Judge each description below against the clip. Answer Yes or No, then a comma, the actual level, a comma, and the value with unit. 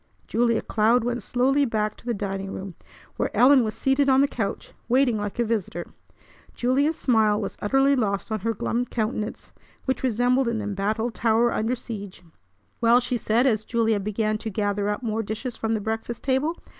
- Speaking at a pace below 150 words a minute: No, average, 180 wpm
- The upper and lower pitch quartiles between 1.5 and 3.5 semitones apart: Yes, average, 2.8 semitones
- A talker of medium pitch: No, high, 225 Hz